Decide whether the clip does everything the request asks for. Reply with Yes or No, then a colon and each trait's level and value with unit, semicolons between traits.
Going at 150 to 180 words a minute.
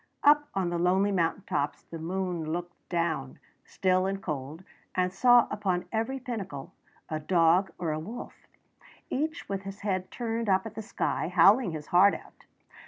Yes: average, 170 wpm